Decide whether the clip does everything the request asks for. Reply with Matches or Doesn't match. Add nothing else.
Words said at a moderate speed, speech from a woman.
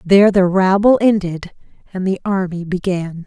Matches